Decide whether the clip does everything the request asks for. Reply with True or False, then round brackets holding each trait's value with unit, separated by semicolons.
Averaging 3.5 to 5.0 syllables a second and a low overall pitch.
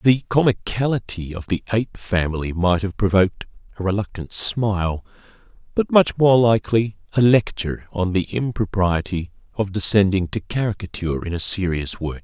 False (5.3 syllables/s; 100 Hz)